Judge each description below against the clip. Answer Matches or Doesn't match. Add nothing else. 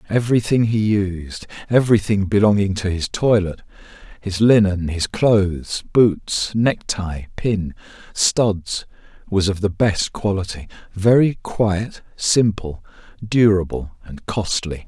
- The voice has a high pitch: Doesn't match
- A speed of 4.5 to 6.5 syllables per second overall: Doesn't match